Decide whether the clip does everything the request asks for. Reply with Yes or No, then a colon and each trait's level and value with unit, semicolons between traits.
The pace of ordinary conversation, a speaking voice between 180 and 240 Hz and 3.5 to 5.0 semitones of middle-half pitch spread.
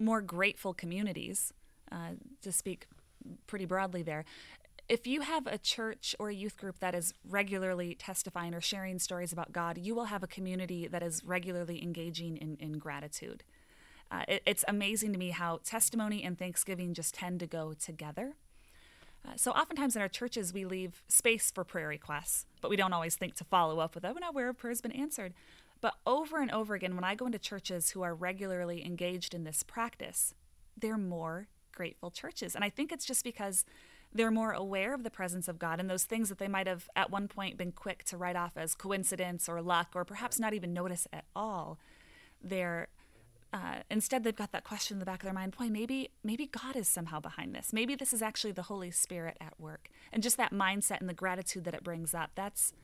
No: fast, 210 wpm; high, 190 Hz; average, 3.9 semitones